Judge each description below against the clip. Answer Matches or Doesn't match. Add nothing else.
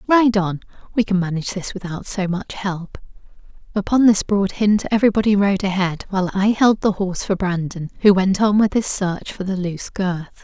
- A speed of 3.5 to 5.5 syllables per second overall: Matches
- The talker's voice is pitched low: Doesn't match